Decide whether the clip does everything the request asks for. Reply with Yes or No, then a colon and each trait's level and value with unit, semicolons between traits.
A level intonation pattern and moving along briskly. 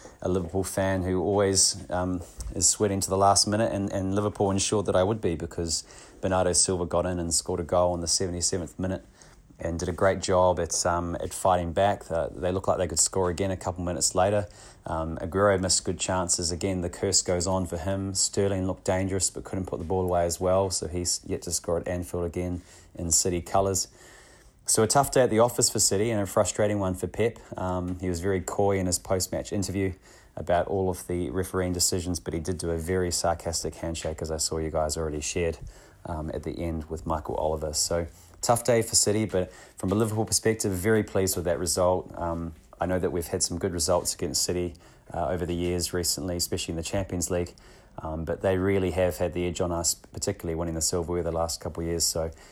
Yes: narrow, 2.1 semitones; fast, 225 wpm